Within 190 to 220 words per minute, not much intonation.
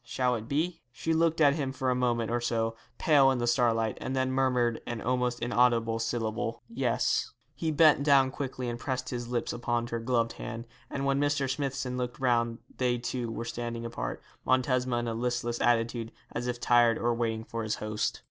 Yes: average, 195 wpm; narrow, 1.9 semitones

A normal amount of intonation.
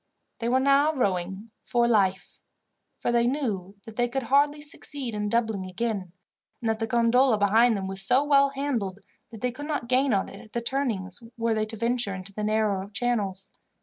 Yes: average, 4.0 semitones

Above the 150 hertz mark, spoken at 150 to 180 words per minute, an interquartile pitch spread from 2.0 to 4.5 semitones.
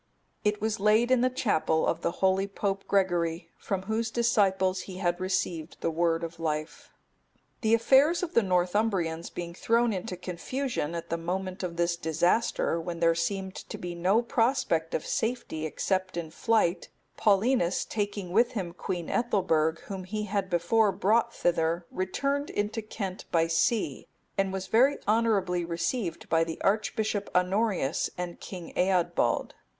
Yes: high, 190 Hz; average, 155 wpm; average, 4.2 semitones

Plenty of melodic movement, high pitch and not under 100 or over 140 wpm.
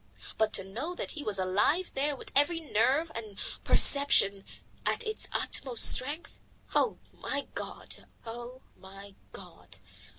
Yes: wide, 6.2 semitones; very high, 255 Hz; slow, 135 wpm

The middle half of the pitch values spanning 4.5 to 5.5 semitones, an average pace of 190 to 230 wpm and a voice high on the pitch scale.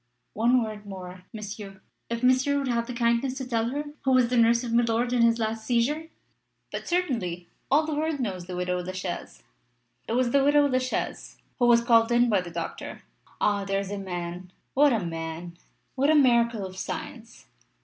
Yes: average, 5.1 semitones; average, 200 wpm; high, 235 Hz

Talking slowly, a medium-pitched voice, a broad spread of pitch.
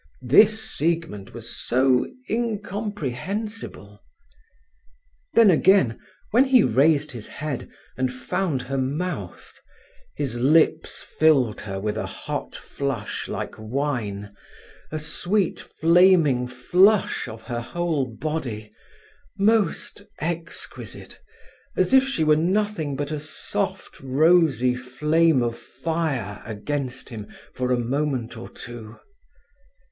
Yes: slow, 110 wpm; medium, 145 Hz; wide, 5.8 semitones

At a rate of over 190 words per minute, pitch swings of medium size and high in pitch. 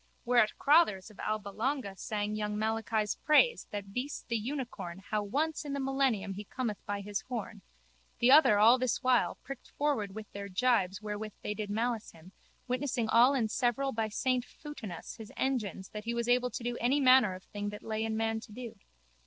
Yes: average, 200 wpm; average, 3.5 semitones; high, 225 Hz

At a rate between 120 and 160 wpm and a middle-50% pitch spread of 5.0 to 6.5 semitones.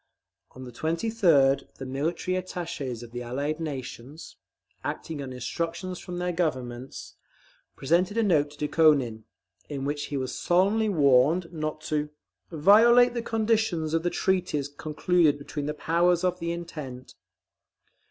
No: average, 140 wpm; average, 4.3 semitones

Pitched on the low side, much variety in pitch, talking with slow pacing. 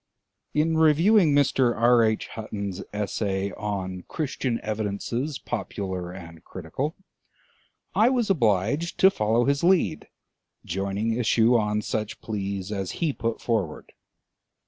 Yes: low, 110 Hz; wide, 6.1 semitones; slow, 120 wpm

